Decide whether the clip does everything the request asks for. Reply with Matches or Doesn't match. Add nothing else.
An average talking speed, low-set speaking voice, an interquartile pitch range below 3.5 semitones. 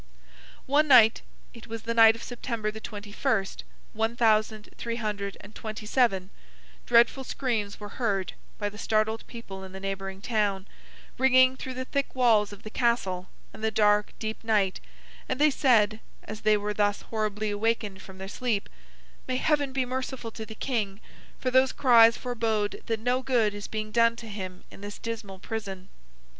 Doesn't match